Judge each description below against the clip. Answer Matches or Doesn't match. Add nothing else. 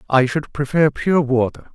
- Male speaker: Matches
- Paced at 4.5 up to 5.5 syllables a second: Matches